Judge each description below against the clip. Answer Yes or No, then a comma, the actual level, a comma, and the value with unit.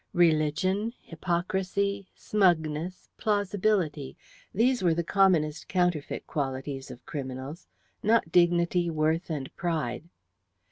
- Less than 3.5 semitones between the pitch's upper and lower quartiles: No, average, 3.8 semitones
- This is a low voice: No, medium, 170 Hz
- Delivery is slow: Yes, slow, 95 wpm